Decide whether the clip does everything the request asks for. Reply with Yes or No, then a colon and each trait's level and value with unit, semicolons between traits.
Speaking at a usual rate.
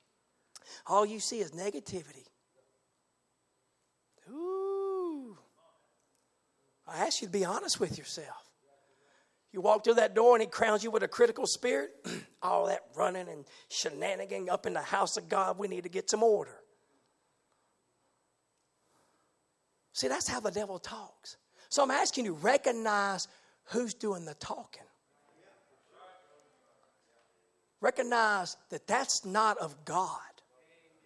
No: slow, 125 wpm